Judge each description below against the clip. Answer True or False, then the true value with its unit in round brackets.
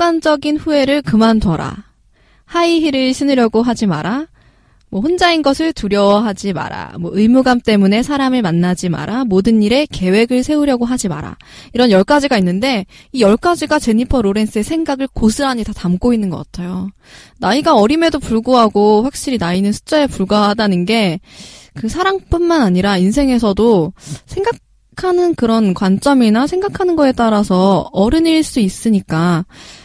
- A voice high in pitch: True (225 Hz)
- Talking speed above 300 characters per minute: True (340 characters per minute)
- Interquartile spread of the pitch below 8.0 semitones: True (6.2 semitones)